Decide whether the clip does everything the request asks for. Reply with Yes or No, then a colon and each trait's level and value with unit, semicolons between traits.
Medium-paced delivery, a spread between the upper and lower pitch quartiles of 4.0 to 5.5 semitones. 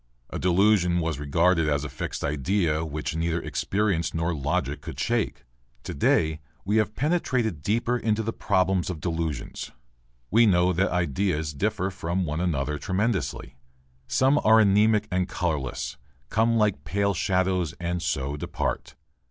Yes: average, 145 wpm; average, 4.7 semitones